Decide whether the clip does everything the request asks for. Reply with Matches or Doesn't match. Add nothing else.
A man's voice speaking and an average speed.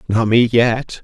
Matches